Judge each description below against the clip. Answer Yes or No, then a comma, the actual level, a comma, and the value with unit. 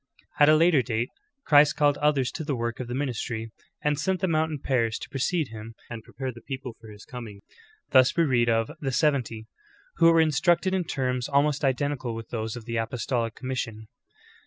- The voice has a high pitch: No, low, 130 Hz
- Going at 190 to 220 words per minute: Yes, fast, 205 wpm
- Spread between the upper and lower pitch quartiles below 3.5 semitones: No, average, 4.2 semitones